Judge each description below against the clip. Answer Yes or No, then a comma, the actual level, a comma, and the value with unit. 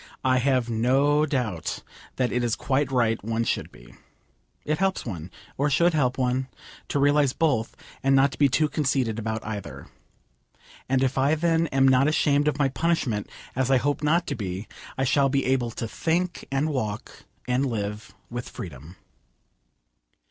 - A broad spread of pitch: No, average, 4.0 semitones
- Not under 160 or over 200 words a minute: Yes, average, 170 wpm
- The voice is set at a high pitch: No, low, 130 Hz